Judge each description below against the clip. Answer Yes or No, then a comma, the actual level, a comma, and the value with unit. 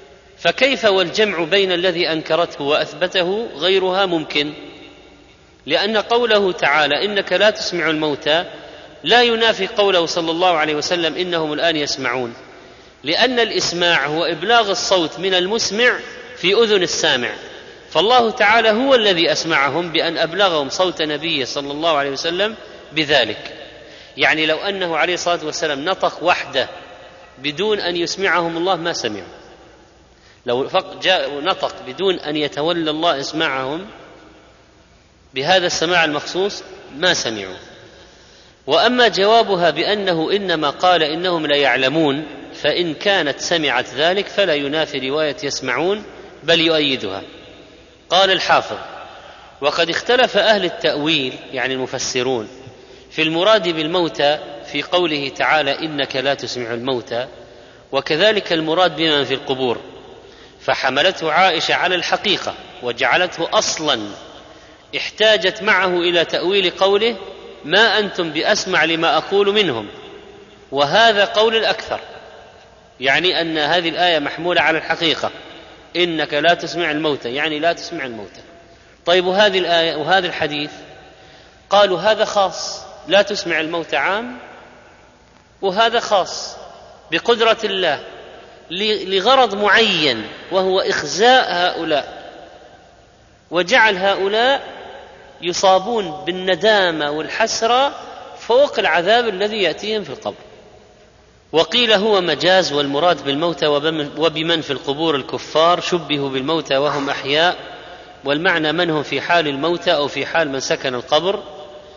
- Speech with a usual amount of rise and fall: Yes, average, 4.7 semitones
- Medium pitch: Yes, medium, 170 Hz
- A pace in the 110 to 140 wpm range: Yes, average, 115 wpm